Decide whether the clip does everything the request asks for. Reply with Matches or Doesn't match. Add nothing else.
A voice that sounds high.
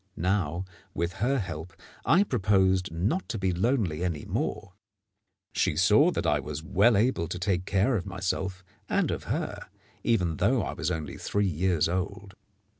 Doesn't match